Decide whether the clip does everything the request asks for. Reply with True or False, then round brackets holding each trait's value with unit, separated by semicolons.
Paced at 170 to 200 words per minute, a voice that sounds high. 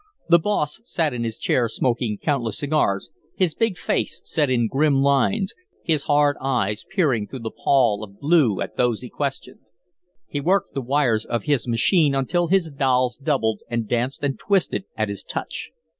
False (175 wpm; 135 Hz)